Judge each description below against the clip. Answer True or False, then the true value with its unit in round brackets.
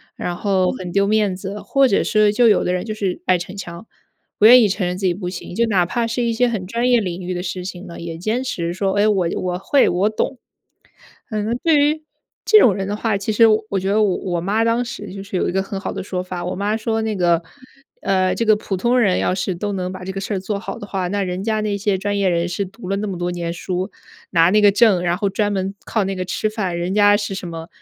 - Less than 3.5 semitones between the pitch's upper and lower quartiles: True (2.9 semitones)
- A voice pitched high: True (195 Hz)